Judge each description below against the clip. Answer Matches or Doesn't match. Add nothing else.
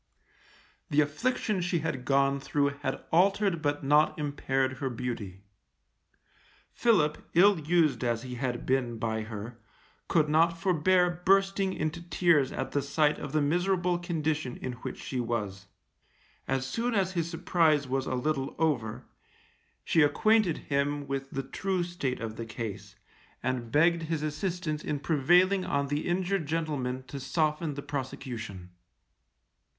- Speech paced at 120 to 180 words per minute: Matches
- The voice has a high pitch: Doesn't match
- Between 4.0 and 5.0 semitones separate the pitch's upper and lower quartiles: Matches